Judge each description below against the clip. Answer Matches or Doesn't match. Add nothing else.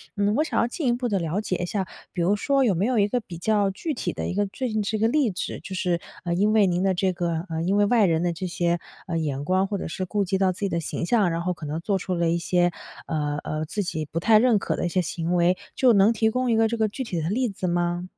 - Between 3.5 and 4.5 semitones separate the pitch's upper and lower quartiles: Matches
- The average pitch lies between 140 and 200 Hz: Matches